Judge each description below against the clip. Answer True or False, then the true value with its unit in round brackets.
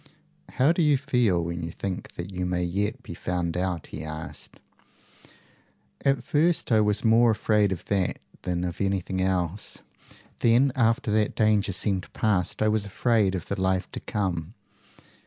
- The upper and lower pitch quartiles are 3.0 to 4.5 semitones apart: True (3.9 semitones)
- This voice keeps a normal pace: True (165 wpm)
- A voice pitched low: True (100 Hz)